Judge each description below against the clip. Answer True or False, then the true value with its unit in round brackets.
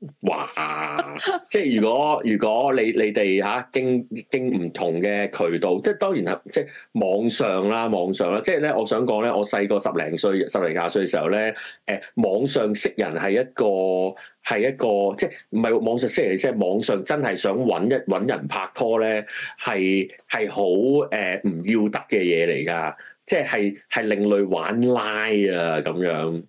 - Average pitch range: True (3.4 semitones)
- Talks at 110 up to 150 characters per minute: False (240 characters per minute)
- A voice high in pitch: False (105 Hz)